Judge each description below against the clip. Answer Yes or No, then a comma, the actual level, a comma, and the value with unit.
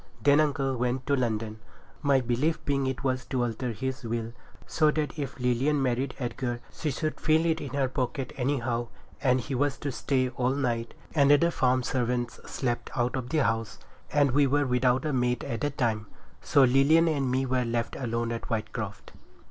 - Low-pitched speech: Yes, low, 130 Hz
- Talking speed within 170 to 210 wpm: Yes, average, 190 wpm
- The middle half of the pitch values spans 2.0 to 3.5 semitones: Yes, average, 2.8 semitones